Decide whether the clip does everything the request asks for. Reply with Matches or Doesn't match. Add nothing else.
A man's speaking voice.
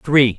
Matches